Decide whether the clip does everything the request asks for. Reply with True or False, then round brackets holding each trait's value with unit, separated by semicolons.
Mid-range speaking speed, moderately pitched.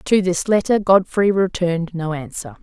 True (160 wpm; 180 Hz)